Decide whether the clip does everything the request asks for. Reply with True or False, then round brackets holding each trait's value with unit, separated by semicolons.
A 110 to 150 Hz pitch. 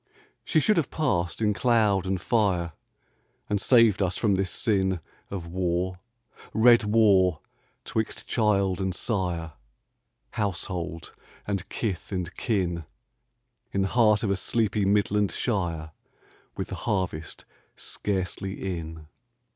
False (95 Hz)